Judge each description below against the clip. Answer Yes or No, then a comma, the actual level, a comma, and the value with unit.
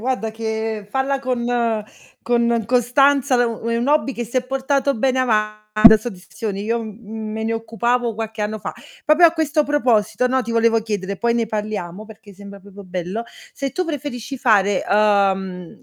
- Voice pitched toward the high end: Yes, high, 225 Hz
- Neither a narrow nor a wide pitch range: Yes, average, 3.0 semitones